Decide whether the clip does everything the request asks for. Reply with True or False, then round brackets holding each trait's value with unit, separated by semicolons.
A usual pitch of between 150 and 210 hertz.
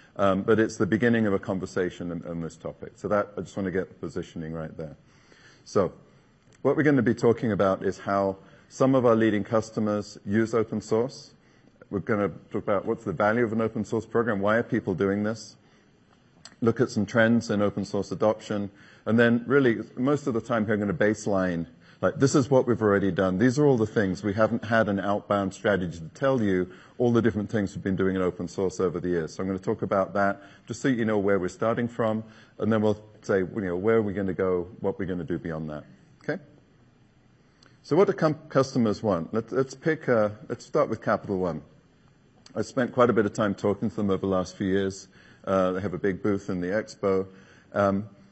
False (105 Hz)